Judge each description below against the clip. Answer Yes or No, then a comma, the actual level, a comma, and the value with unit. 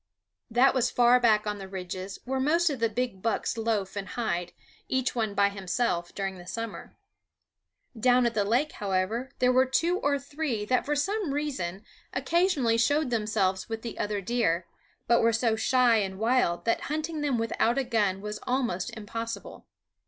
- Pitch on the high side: Yes, high, 230 Hz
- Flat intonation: No, average, 4.3 semitones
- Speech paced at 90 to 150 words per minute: No, average, 175 wpm